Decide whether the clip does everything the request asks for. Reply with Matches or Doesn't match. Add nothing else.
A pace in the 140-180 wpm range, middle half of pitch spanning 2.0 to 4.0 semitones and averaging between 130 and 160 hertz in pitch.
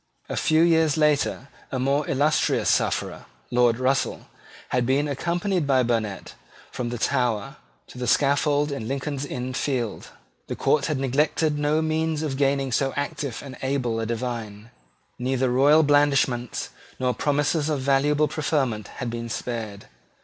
Matches